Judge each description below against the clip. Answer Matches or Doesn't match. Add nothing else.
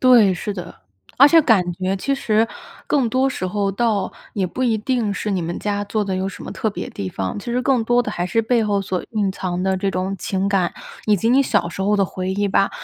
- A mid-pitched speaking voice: Doesn't match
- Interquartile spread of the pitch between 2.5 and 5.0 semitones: Matches